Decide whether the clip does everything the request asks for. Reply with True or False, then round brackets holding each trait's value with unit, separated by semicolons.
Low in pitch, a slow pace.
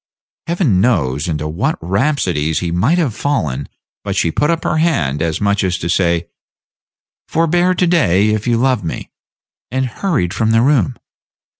False (110 Hz; 165 wpm)